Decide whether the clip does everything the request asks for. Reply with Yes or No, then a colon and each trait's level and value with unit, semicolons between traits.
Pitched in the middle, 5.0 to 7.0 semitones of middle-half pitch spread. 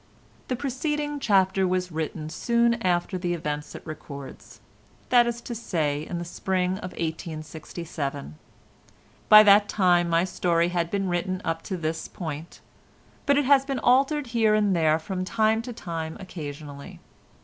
Yes: medium, 180 Hz; wide, 5.6 semitones